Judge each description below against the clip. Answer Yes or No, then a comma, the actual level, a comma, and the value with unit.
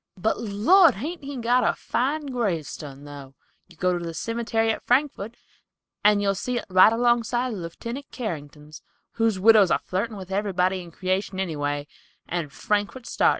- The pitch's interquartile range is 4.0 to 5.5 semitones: Yes, average, 5.1 semitones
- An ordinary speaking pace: Yes, average, 170 wpm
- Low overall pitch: No, high, 205 Hz